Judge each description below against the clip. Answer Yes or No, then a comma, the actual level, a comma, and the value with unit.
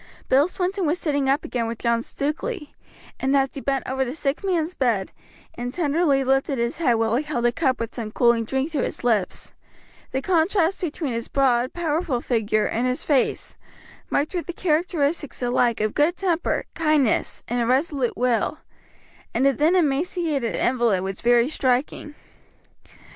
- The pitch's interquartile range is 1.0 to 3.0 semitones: No, average, 4.8 semitones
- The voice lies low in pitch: No, very high, 270 Hz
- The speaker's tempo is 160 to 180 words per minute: Yes, average, 170 wpm